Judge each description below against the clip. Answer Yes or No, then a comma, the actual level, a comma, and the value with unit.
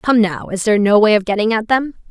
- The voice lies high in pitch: Yes, high, 215 Hz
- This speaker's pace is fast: Yes, fast, 285 wpm